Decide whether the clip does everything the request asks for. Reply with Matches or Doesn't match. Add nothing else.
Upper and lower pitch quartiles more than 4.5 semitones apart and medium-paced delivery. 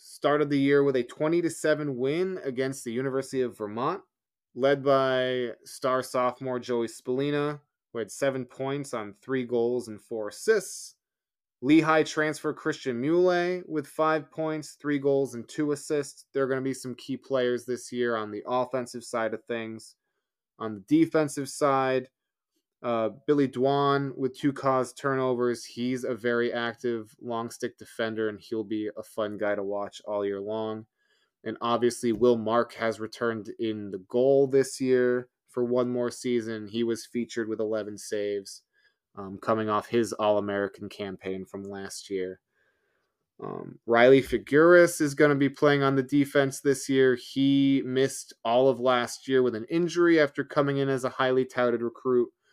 Doesn't match